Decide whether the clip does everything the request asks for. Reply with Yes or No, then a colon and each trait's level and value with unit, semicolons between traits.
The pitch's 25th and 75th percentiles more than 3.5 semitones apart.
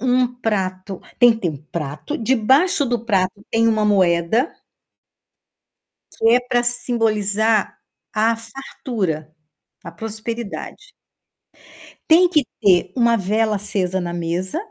Yes: average, 4.5 semitones